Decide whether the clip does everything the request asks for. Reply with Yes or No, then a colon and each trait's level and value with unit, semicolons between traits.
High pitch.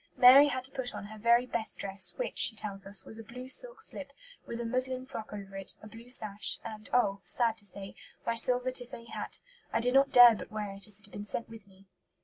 Yes: high, 230 Hz